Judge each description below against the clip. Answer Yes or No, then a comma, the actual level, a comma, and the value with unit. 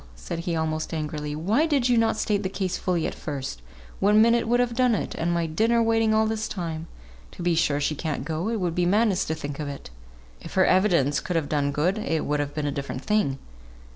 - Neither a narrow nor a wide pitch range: No, wide, 6.1 semitones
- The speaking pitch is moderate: Yes, medium, 175 Hz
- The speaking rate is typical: No, fast, 235 wpm